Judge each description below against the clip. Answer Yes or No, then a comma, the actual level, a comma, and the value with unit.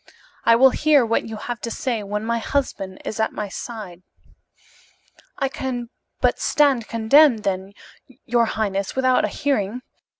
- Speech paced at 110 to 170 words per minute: Yes, average, 155 wpm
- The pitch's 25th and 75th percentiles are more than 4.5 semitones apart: No, average, 3.7 semitones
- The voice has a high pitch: Yes, high, 230 Hz